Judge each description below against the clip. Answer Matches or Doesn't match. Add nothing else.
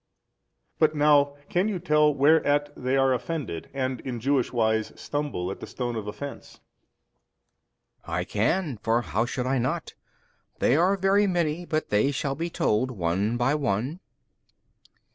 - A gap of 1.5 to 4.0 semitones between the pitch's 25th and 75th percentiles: Doesn't match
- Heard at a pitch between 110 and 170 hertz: Matches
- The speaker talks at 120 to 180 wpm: Matches